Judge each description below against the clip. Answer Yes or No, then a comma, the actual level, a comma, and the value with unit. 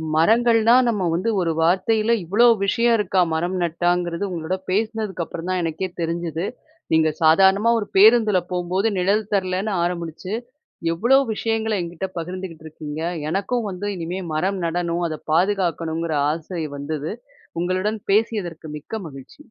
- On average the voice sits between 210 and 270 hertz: No, medium, 185 Hz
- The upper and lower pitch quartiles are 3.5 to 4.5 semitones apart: Yes, average, 4.0 semitones